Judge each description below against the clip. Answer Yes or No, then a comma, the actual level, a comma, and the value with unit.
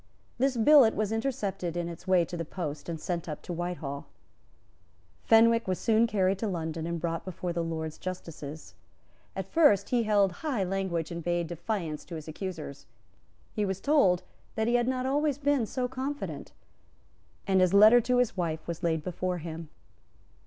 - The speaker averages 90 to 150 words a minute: No, average, 175 wpm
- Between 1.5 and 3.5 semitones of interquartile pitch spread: No, average, 5.1 semitones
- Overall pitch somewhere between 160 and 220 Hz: Yes, medium, 185 Hz